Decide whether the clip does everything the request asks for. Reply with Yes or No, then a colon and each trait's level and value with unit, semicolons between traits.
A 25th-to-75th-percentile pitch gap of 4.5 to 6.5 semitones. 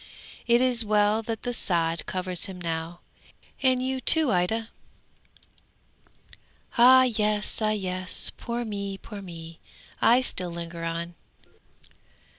Yes: average, 5.2 semitones